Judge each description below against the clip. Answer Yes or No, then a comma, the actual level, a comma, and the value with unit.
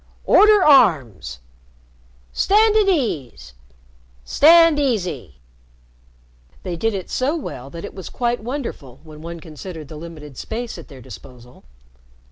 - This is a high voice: No, medium, 175 Hz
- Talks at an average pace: No, slow, 125 wpm